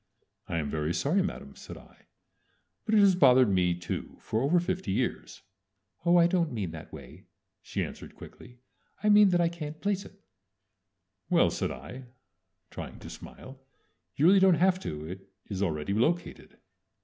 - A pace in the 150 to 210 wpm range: Yes, average, 170 wpm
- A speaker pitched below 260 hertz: Yes, medium, 140 Hz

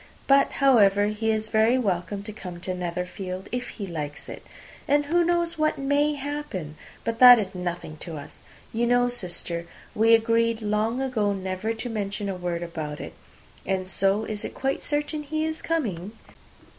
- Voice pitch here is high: Yes, high, 215 Hz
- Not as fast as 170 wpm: No, average, 175 wpm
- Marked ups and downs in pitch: Yes, wide, 5.8 semitones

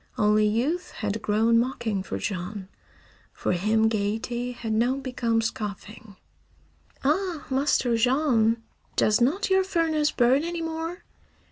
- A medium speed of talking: No, slow, 125 wpm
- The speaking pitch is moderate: No, high, 235 Hz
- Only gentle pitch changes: No, wide, 5.5 semitones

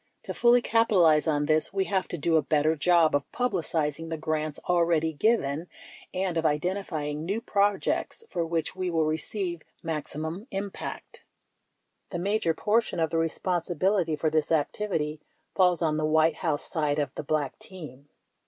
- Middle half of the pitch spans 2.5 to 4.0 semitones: Yes, average, 3.4 semitones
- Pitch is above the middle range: No, medium, 165 Hz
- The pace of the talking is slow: No, average, 160 wpm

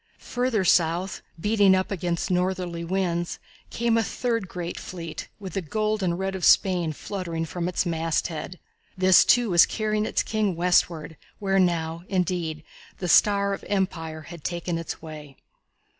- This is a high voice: No, medium, 180 Hz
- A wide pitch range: No, average, 2.8 semitones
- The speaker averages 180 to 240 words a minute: No, average, 155 wpm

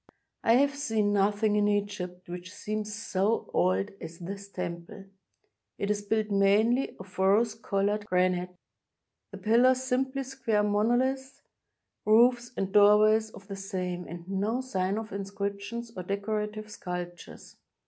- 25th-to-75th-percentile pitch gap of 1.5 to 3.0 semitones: Yes, narrow, 2.6 semitones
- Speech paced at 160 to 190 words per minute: No, slow, 135 wpm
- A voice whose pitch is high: Yes, high, 205 Hz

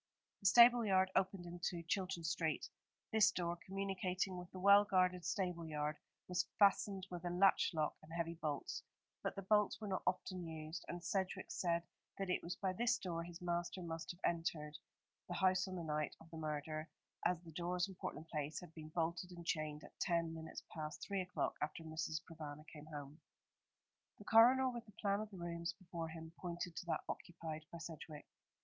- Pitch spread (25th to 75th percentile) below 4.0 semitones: Yes, average, 2.7 semitones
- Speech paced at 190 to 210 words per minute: Yes, average, 195 wpm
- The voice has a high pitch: No, medium, 175 Hz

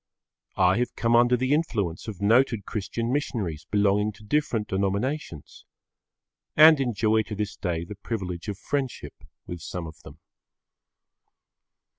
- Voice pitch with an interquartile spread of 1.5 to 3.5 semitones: No, average, 4.3 semitones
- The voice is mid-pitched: No, low, 105 Hz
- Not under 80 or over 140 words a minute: Yes, slow, 135 wpm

